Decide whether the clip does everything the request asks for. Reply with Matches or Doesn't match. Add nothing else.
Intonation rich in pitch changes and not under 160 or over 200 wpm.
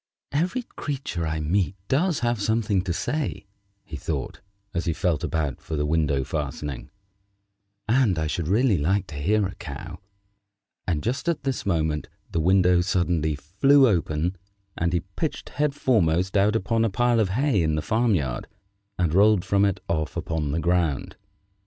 Matches